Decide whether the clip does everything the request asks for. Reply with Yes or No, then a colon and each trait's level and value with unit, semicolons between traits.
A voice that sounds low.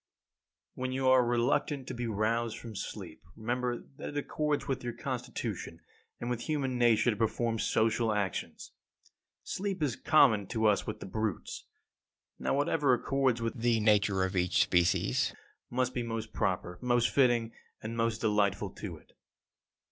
Yes: low, 115 Hz